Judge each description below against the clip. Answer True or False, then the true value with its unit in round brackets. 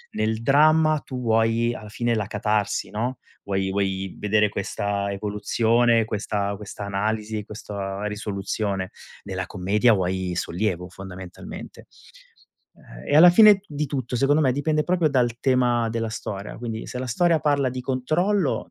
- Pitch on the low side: True (110 Hz)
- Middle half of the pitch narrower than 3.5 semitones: False (4.3 semitones)